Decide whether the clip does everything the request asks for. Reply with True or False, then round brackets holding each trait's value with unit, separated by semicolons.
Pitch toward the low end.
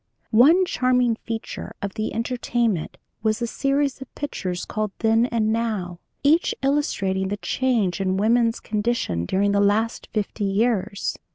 False (225 Hz)